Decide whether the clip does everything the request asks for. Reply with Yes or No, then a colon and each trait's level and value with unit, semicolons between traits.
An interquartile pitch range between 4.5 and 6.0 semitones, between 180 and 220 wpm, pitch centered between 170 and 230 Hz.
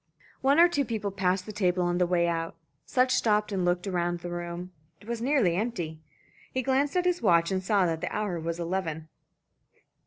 Yes: average, 4.8 semitones; fast, 205 wpm; medium, 185 Hz